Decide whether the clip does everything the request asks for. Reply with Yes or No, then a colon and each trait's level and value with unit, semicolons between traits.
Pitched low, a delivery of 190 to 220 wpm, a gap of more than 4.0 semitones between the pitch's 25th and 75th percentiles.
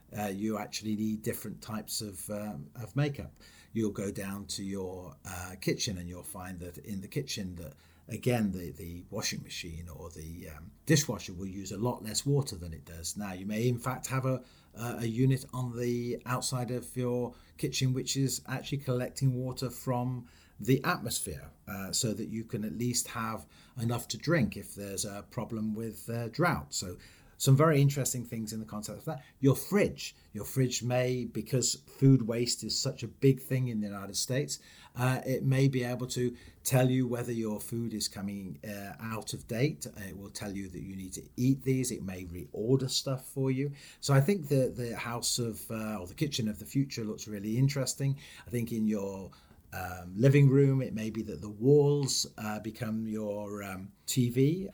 Yes: low, 115 Hz; average, 195 wpm; average, 4.5 semitones